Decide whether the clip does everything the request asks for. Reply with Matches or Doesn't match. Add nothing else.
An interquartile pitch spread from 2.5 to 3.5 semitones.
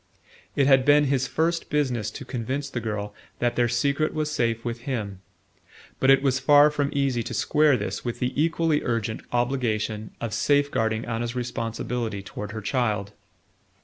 Doesn't match